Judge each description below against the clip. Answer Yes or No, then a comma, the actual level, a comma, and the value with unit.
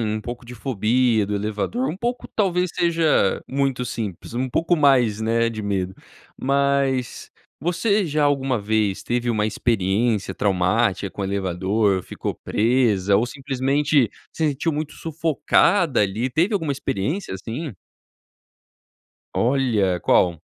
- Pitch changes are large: Yes, wide, 5.7 semitones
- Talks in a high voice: No, low, 120 Hz